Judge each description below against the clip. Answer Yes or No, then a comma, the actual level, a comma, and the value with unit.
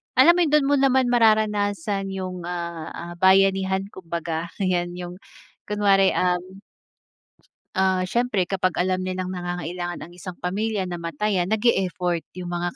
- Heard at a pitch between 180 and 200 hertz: Yes, medium, 185 Hz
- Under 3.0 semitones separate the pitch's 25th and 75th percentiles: Yes, narrow, 2.5 semitones